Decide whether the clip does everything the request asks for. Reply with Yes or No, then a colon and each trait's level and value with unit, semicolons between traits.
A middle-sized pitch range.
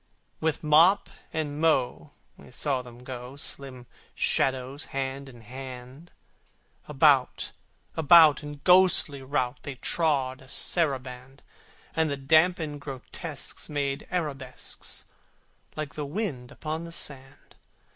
Yes: average, 3.2 semitones